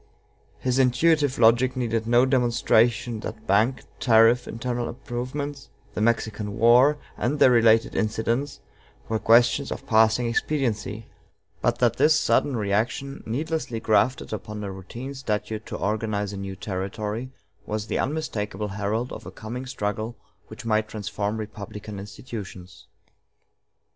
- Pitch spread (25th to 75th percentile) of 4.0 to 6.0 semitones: No, average, 3.0 semitones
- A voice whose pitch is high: No, low, 115 Hz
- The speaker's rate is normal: No, slow, 130 wpm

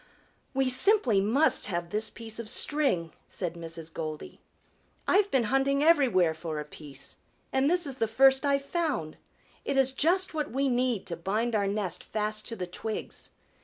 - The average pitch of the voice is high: Yes, high, 230 Hz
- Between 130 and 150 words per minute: No, average, 170 wpm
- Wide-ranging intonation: Yes, wide, 7.6 semitones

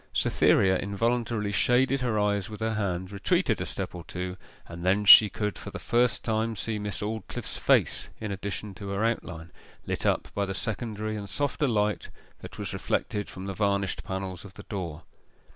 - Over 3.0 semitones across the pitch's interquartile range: No, average, 2.7 semitones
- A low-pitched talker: Yes, low, 105 Hz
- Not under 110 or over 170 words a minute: No, average, 185 wpm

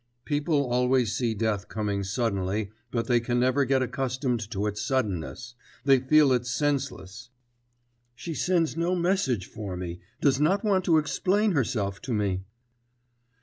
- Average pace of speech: Yes, average, 150 wpm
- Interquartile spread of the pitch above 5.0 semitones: Yes, wide, 5.5 semitones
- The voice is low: Yes, low, 125 Hz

